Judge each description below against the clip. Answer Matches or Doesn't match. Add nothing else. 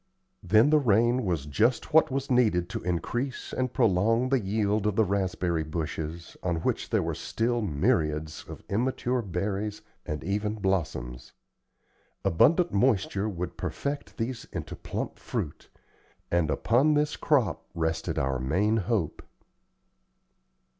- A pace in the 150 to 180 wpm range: Doesn't match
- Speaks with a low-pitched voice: Matches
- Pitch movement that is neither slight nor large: Doesn't match